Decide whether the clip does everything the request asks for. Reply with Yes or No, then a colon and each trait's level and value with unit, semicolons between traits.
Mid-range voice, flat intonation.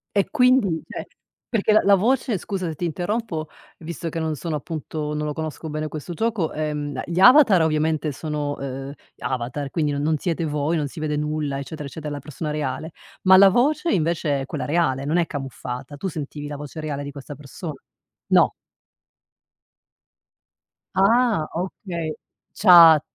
No: medium, 155 Hz; average, 3.4 semitones